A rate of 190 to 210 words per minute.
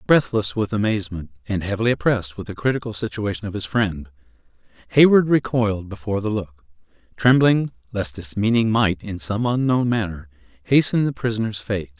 No: average, 155 wpm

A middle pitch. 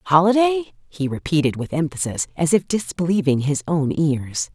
Yes: medium, 165 Hz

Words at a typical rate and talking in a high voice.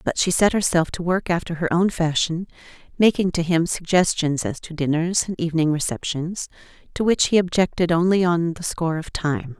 No: average, 190 wpm; medium, 170 Hz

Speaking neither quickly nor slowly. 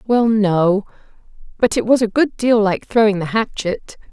Yes: average, 175 wpm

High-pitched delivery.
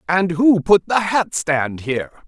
No: medium, 175 Hz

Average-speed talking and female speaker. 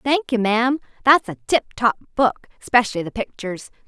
Yes: average, 170 wpm; female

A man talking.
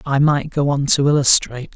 Yes: male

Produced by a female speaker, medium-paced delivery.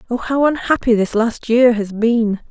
Yes: female; average, 190 wpm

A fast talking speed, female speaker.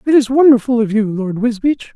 No: fast, 215 wpm; male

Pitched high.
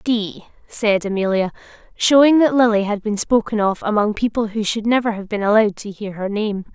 Yes: high, 215 Hz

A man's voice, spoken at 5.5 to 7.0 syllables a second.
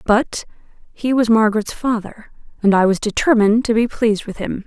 No: female; 5.6 syllables/s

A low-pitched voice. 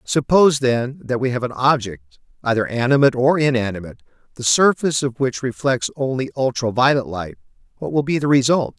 Yes: low, 130 Hz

